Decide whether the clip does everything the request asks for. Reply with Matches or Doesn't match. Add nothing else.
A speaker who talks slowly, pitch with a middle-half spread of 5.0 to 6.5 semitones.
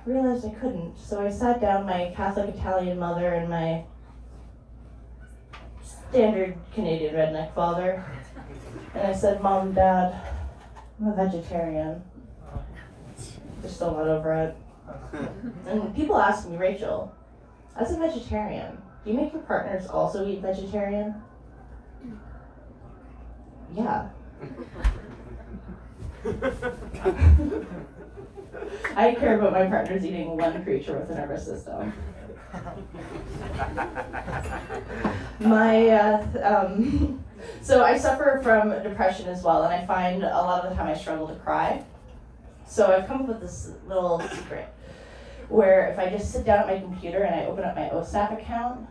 Doesn't match